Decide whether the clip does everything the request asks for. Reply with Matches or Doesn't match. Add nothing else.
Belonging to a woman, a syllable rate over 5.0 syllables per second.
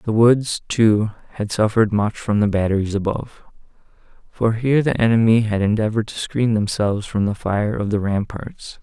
Doesn't match